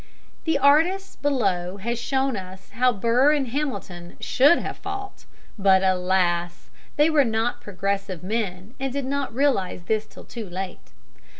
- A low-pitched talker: No, high, 225 Hz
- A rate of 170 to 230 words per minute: No, average, 140 wpm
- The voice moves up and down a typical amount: No, wide, 6.8 semitones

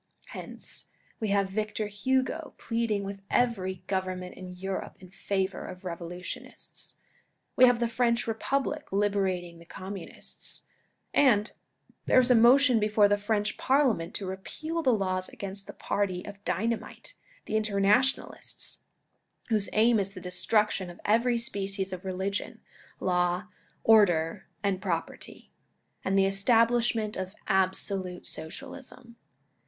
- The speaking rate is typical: No, slow, 130 wpm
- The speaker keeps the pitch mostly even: No, average, 3.6 semitones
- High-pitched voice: Yes, high, 200 Hz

